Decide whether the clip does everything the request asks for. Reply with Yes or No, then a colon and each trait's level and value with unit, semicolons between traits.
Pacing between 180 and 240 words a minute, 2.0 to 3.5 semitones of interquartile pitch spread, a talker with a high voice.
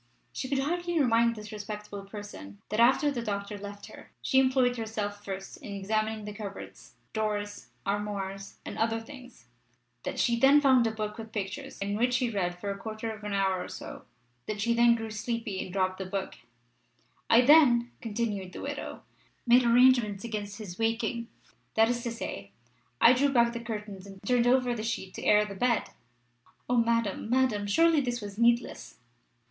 Yes: average, 185 wpm; average, 2.9 semitones; high, 220 Hz